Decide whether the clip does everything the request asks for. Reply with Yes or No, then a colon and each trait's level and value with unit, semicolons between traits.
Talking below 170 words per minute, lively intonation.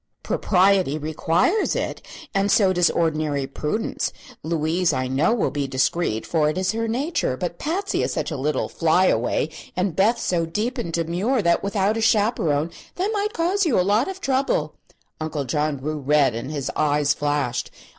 No: average, 175 wpm; wide, 6.6 semitones